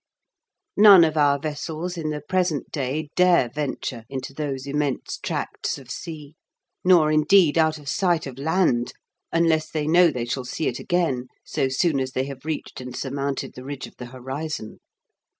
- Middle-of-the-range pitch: Yes, medium, 150 Hz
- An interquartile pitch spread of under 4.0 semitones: Yes, average, 3.4 semitones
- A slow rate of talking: No, average, 170 wpm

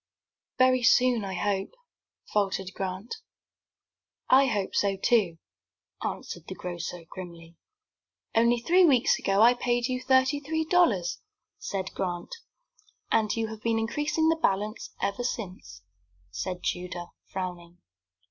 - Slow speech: Yes, slow, 125 wpm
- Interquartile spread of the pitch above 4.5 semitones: Yes, wide, 5.5 semitones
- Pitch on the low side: No, high, 210 Hz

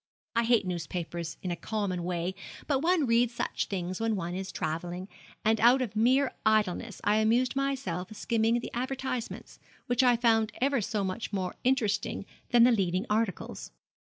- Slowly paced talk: No, average, 165 wpm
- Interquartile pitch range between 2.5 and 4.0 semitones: No, average, 4.8 semitones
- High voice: Yes, high, 220 Hz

